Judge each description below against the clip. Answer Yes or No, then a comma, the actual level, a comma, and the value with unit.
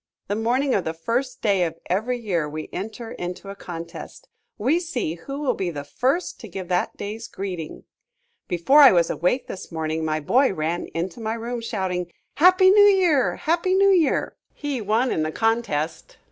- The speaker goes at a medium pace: Yes, average, 185 wpm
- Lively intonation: Yes, wide, 7.4 semitones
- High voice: Yes, high, 215 Hz